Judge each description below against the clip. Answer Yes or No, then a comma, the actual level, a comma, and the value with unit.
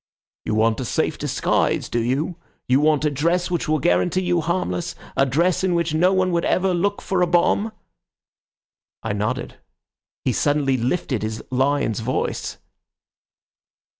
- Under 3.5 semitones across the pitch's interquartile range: No, wide, 5.6 semitones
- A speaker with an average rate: Yes, average, 155 wpm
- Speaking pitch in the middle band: Yes, medium, 155 Hz